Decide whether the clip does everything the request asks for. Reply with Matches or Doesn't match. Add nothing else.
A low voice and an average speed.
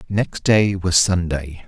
Matches